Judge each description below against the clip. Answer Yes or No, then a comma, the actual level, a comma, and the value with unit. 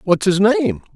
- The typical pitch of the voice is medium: Yes, medium, 175 Hz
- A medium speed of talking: Yes, average, 190 wpm